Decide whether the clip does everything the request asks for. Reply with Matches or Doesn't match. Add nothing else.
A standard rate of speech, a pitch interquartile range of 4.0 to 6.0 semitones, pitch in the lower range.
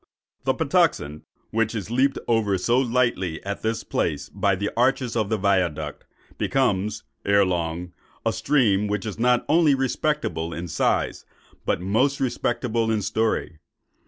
Matches